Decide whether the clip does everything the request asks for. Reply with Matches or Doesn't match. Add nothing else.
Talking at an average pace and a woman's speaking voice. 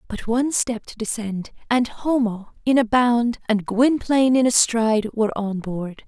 Matches